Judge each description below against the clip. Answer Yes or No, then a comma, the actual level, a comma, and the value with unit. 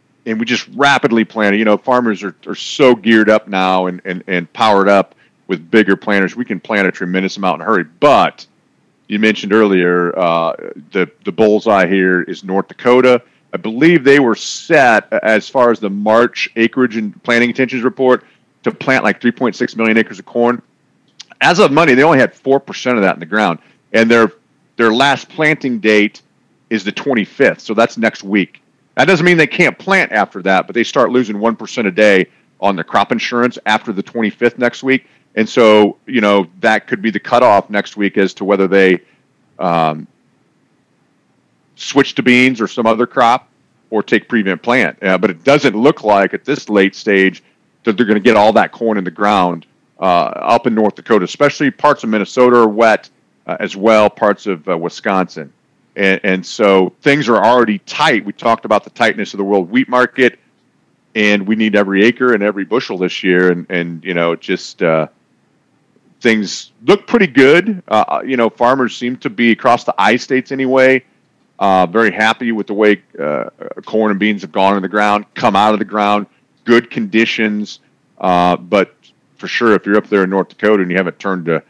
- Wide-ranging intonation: No, average, 3.9 semitones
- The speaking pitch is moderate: No, low, 110 Hz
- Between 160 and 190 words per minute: No, average, 200 wpm